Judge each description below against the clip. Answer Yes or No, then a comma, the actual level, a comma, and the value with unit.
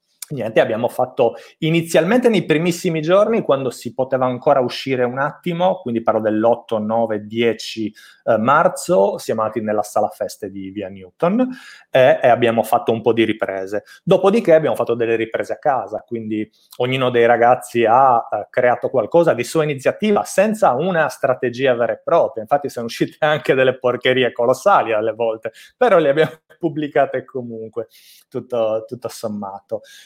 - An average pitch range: No, wide, 5.8 semitones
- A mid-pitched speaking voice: No, low, 125 Hz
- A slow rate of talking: No, average, 150 wpm